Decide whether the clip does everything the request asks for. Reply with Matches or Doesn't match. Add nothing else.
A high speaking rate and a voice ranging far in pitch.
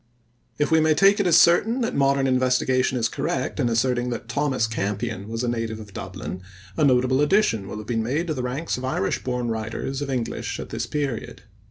Doesn't match